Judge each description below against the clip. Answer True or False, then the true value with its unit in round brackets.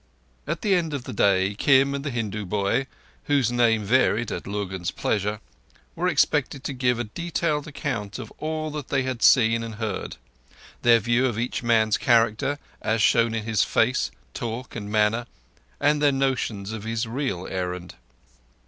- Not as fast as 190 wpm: True (160 wpm)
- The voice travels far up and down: False (4.2 semitones)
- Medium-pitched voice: False (115 Hz)